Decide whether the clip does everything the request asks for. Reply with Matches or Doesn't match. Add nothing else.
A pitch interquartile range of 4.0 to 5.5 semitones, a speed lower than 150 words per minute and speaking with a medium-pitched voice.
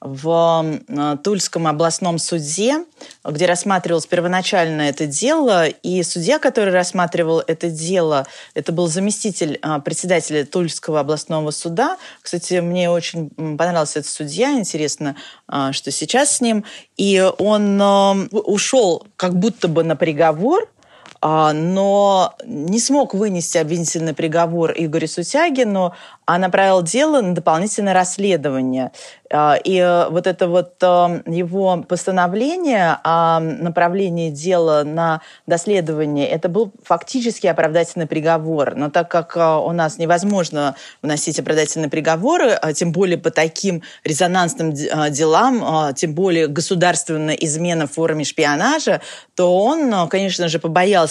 Doesn't match